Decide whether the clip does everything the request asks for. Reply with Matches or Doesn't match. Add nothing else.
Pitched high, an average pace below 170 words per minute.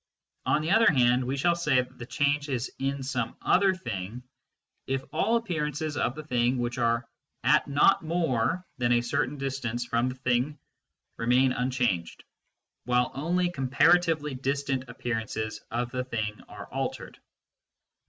Doesn't match